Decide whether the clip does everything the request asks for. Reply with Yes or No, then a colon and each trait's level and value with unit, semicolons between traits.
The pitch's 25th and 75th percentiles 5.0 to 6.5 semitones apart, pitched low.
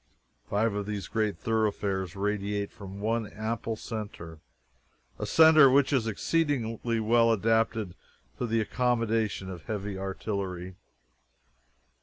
No: narrow, 2.4 semitones; low, 110 Hz